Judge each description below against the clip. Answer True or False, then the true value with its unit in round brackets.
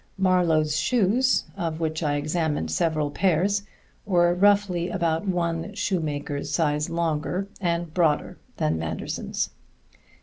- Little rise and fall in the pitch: False (3.2 semitones)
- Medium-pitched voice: True (170 Hz)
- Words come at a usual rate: False (110 wpm)